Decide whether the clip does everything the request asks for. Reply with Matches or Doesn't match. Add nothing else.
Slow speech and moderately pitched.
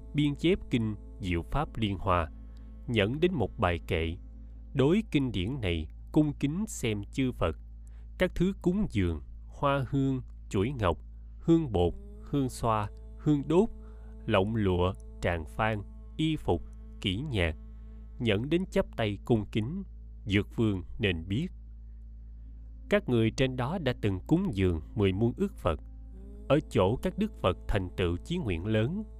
Doesn't match